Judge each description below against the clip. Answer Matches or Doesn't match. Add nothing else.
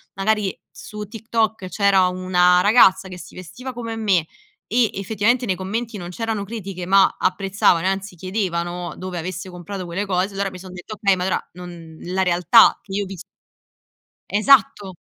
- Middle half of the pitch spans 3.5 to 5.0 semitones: Doesn't match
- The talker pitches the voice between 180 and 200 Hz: Matches